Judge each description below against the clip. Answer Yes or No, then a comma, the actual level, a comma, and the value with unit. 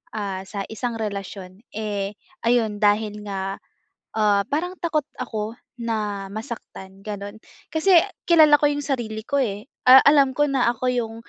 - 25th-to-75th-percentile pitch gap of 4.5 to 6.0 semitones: Yes, average, 4.8 semitones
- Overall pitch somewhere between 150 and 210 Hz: No, high, 220 Hz